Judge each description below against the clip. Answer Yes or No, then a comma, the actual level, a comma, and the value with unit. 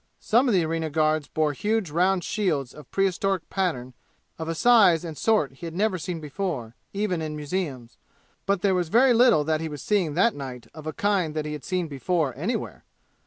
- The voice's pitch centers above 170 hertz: No, medium, 165 Hz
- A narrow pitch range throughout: No, average, 4.4 semitones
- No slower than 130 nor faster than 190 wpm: No, fast, 205 wpm